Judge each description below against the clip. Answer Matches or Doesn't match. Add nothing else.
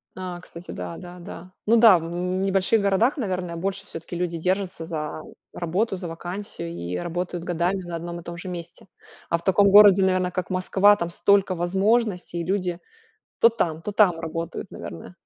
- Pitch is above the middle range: Doesn't match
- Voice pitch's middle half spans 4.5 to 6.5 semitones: Doesn't match